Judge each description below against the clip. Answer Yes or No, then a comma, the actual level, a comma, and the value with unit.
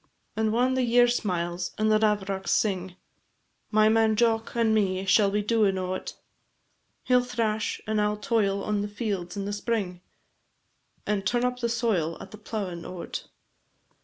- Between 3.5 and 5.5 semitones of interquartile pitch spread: No, average, 2.8 semitones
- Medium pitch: No, high, 210 Hz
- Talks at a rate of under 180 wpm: Yes, average, 170 wpm